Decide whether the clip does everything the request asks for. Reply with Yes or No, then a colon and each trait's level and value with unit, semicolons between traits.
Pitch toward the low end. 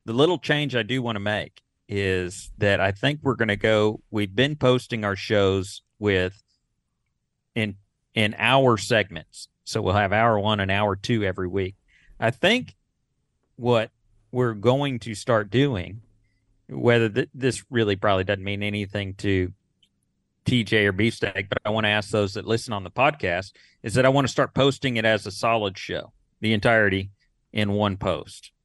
Yes: low, 105 Hz